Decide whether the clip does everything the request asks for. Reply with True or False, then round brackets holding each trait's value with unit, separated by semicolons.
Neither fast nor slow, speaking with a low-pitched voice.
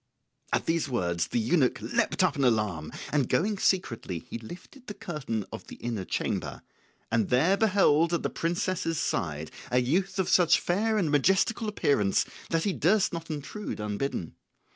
False (165 wpm; 160 Hz)